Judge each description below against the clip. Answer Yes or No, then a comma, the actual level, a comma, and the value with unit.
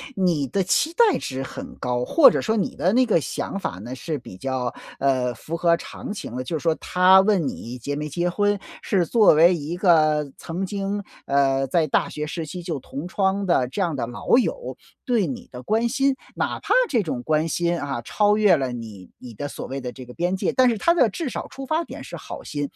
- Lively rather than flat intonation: Yes, wide, 6.8 semitones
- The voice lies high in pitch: No, medium, 165 Hz